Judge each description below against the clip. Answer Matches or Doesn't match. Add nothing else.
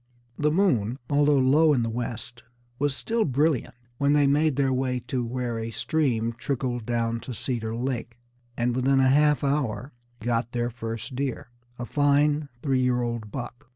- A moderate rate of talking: Matches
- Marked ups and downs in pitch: Doesn't match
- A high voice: Doesn't match